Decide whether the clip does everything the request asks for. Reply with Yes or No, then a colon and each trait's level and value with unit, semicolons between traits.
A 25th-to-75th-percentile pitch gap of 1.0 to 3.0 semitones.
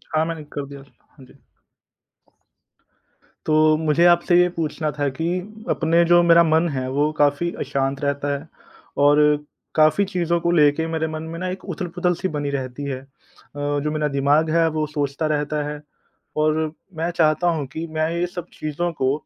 Yes: narrow, 2.6 semitones